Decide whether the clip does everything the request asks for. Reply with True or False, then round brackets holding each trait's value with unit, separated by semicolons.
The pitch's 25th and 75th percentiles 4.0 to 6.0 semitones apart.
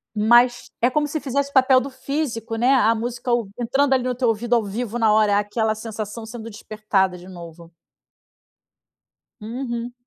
False (2.9 semitones)